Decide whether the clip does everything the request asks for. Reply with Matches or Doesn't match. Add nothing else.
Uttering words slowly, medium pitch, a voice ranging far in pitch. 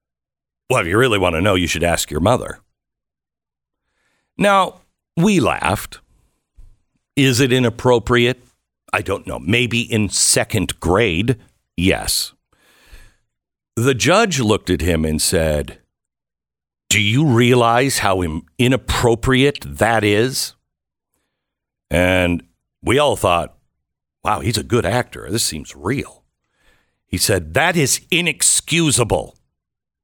Doesn't match